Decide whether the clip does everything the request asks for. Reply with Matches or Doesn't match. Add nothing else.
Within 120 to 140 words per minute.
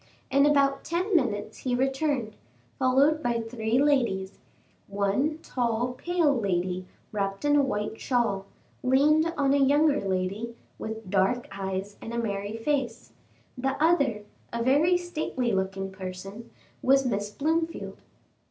Matches